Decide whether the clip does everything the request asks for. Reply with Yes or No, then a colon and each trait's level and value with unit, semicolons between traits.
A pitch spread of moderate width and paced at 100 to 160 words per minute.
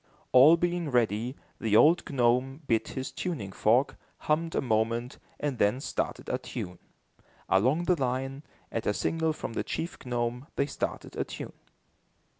Yes: average, 4.5 semitones; average, 155 wpm